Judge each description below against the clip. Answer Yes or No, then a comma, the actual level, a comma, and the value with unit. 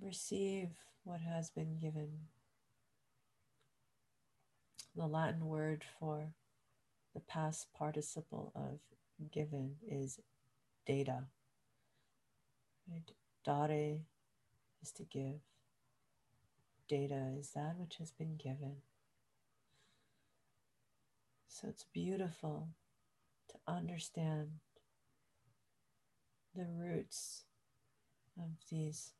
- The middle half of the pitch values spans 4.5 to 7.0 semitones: No, average, 3.8 semitones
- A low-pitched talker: No, medium, 145 Hz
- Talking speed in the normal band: No, slow, 75 wpm